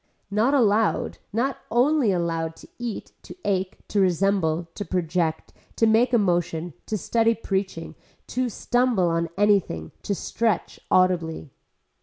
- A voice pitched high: Yes, high, 195 Hz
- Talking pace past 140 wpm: No, slow, 135 wpm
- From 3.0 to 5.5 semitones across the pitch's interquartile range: Yes, average, 4.9 semitones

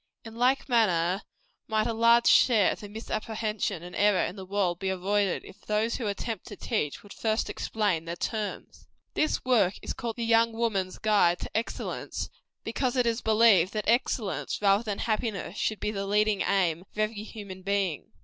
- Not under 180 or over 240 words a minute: Yes, average, 185 wpm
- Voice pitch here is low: No, high, 210 Hz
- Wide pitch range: No, average, 2.7 semitones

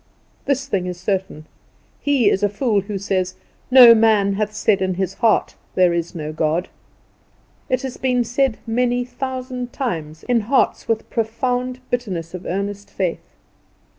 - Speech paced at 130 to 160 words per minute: Yes, average, 155 wpm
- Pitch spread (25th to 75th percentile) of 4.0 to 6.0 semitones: Yes, average, 4.9 semitones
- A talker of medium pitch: No, high, 215 Hz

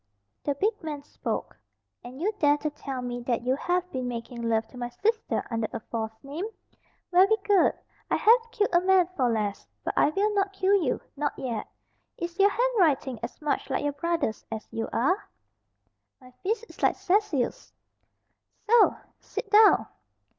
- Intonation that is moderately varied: No, wide, 8.1 semitones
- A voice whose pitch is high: Yes, very high, 295 Hz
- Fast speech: No, average, 175 wpm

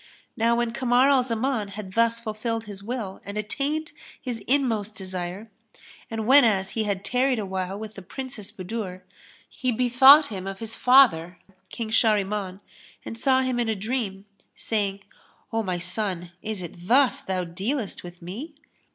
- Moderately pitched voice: No, high, 220 Hz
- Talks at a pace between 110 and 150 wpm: No, average, 160 wpm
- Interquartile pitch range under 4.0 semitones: No, average, 4.4 semitones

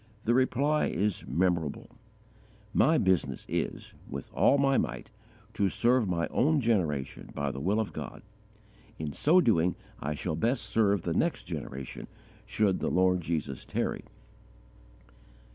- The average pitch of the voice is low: Yes, very low, 95 Hz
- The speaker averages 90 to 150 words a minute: Yes, average, 145 wpm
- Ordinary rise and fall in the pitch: No, wide, 6.6 semitones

